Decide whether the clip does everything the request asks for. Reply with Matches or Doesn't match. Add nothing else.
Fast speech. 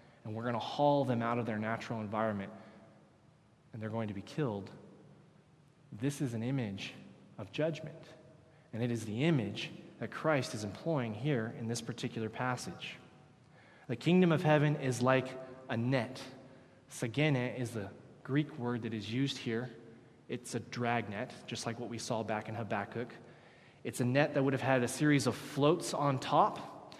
Doesn't match